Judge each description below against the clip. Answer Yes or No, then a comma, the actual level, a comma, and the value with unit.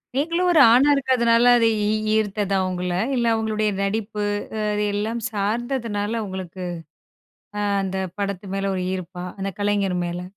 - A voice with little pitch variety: No, average, 3.2 semitones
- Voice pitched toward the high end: Yes, high, 205 Hz